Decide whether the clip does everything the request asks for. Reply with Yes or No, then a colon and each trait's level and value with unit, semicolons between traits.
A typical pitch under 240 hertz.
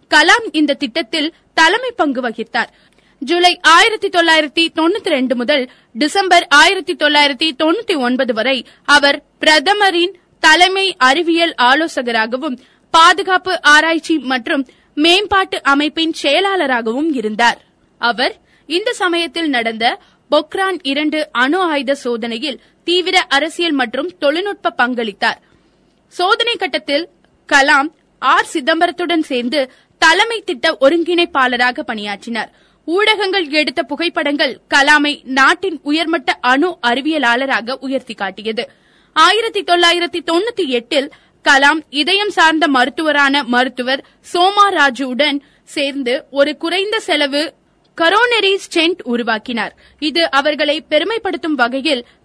No: very high, 310 Hz